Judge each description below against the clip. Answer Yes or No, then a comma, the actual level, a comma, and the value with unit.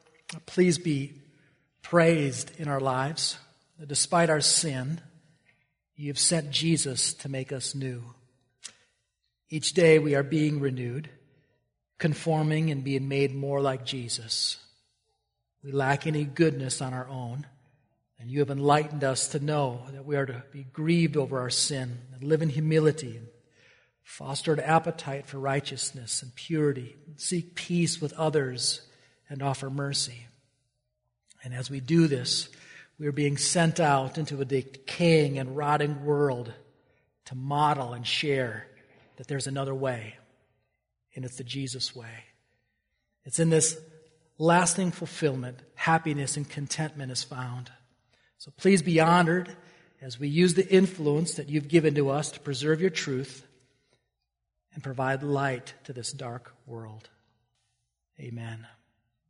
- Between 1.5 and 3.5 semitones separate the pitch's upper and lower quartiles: Yes, average, 3.2 semitones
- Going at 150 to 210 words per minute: No, average, 140 wpm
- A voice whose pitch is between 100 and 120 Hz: No, medium, 140 Hz